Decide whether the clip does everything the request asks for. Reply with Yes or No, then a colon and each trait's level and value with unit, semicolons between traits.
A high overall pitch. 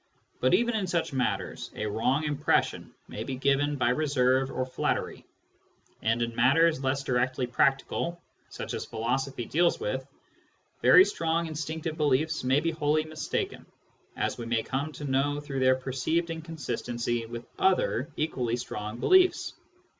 No: low, 135 Hz